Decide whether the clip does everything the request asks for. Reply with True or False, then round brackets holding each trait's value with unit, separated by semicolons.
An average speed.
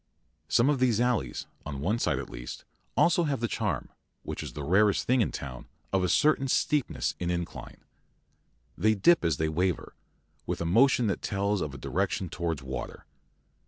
True (180 wpm)